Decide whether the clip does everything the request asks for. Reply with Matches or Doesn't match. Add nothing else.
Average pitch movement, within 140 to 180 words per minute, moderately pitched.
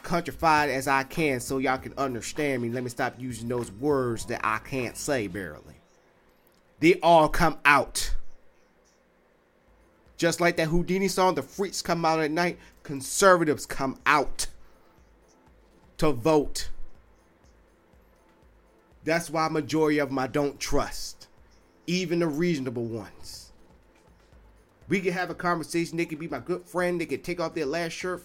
Doesn't match